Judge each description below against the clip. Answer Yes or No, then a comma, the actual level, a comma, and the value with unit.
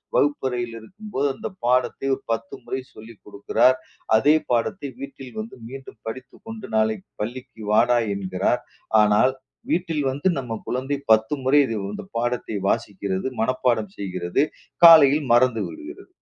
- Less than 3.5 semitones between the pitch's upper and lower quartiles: No, average, 4.6 semitones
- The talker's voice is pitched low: Yes, low, 125 Hz